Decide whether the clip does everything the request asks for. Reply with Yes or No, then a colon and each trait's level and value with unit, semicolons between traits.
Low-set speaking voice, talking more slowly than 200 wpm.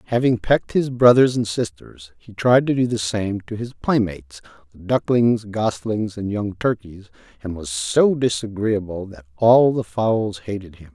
Yes: low, 110 Hz; average, 170 wpm